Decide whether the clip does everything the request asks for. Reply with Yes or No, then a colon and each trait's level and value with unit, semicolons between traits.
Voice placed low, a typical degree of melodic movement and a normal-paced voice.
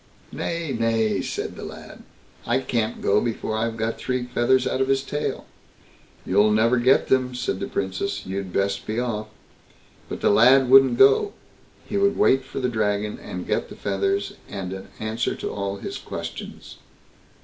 Yes: low, 115 Hz; average, 4.2 semitones; average, 170 wpm